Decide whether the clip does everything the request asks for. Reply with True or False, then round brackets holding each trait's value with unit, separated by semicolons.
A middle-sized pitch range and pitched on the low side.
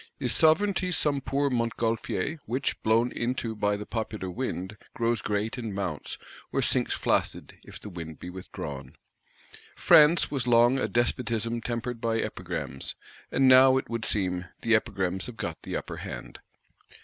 True (3.9 semitones; 115 Hz)